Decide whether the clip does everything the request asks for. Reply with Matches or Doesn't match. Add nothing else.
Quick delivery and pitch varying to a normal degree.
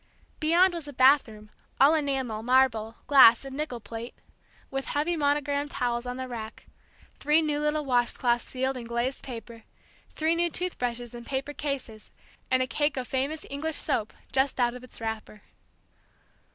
Doesn't match